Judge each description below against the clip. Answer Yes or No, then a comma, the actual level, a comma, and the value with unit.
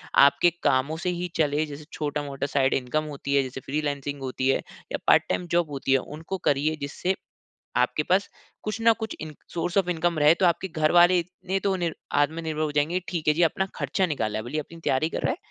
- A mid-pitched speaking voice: Yes, medium, 155 Hz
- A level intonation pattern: No, average, 3.6 semitones